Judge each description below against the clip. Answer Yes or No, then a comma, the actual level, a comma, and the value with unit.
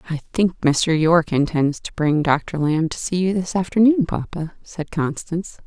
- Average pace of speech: Yes, average, 180 wpm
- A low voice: No, medium, 170 Hz